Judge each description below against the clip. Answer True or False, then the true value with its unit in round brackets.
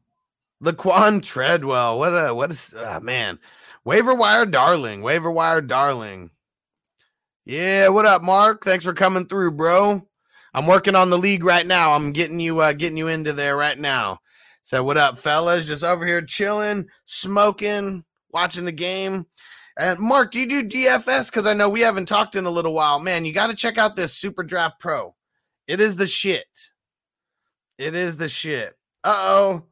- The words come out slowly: False (180 wpm)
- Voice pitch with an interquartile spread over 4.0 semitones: False (3.6 semitones)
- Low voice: False (185 Hz)